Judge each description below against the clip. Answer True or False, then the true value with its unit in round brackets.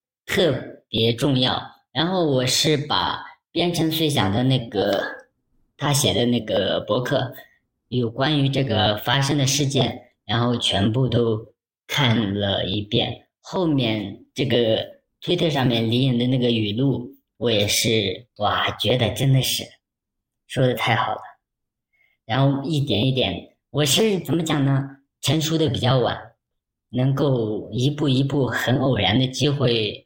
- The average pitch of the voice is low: True (125 Hz)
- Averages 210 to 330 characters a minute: False (200 characters per minute)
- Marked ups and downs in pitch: False (3.6 semitones)